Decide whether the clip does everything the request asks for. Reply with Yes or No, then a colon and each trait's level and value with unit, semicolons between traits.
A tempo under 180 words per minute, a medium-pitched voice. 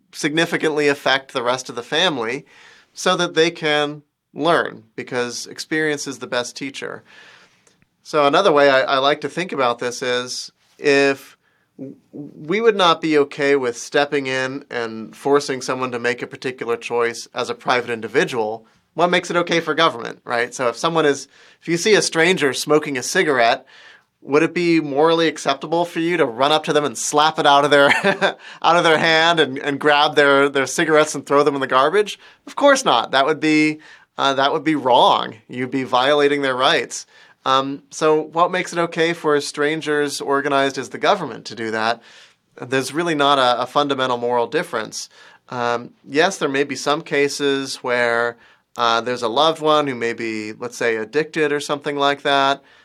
No: average, 185 wpm; medium, 145 Hz